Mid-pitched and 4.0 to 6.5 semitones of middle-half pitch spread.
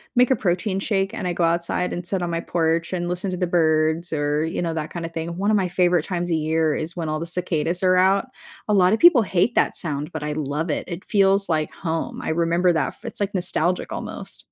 No: medium, 175 Hz; narrow, 2.5 semitones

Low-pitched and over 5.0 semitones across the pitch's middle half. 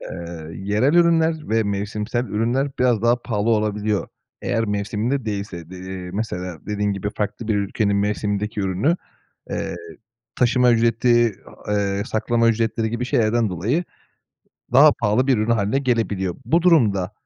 No: low, 110 Hz; average, 2.9 semitones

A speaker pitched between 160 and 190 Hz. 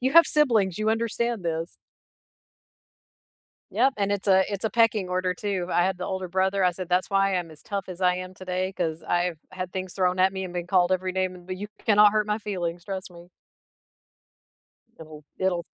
Yes: medium, 185 Hz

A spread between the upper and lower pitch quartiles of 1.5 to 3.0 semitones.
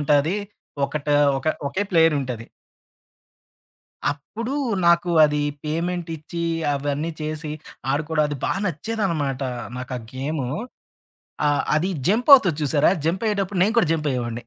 No: average, 3.7 semitones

